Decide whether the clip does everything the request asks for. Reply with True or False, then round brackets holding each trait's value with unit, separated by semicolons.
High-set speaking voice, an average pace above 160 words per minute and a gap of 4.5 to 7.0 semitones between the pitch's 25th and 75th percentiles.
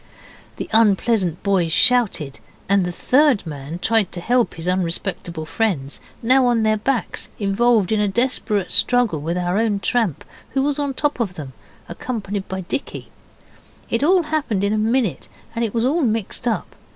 True (215 Hz; 170 wpm; 5.2 semitones)